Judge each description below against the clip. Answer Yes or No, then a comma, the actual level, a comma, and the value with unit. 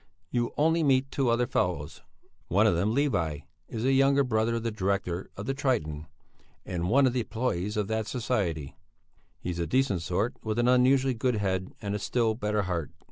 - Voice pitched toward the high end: No, low, 110 Hz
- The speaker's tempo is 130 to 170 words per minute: No, average, 190 wpm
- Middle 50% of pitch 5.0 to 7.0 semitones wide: Yes, wide, 5.5 semitones